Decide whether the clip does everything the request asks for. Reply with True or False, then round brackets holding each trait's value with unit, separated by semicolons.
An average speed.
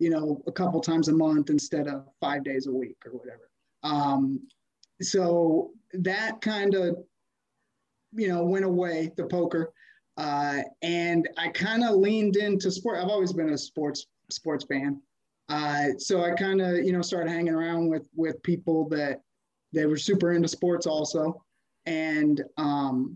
True (165 wpm)